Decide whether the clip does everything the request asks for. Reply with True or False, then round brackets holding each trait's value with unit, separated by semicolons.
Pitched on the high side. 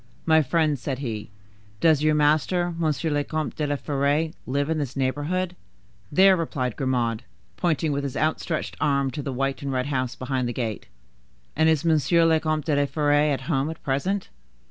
False (145 Hz)